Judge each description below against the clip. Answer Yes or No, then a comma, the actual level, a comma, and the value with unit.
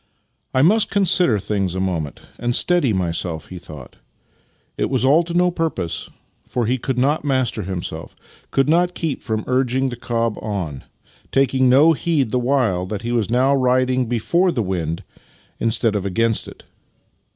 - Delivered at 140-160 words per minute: No, average, 175 wpm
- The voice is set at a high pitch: No, low, 120 Hz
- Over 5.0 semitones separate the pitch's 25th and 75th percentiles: Yes, wide, 5.6 semitones